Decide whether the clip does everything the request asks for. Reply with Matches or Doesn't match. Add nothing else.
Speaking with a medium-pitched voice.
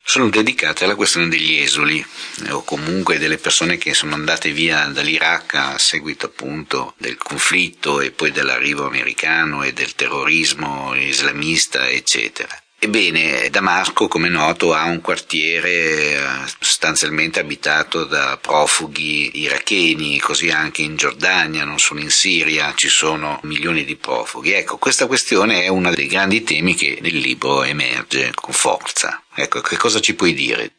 Doesn't match